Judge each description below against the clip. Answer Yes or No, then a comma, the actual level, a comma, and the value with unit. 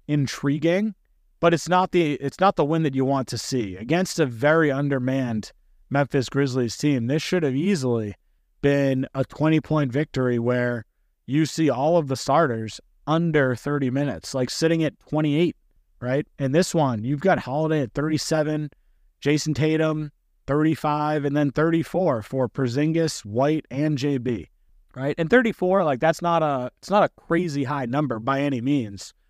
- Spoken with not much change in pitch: No, average, 3.3 semitones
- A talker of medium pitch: Yes, medium, 145 Hz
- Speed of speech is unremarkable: Yes, average, 165 wpm